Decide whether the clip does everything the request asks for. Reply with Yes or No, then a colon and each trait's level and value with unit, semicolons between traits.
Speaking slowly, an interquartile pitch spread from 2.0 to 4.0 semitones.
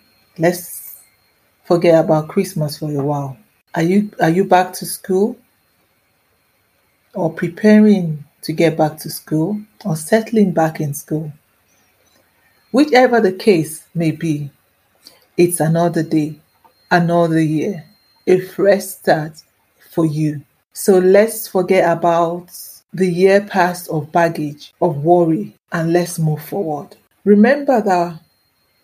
Yes: slow, 120 wpm; average, 3.4 semitones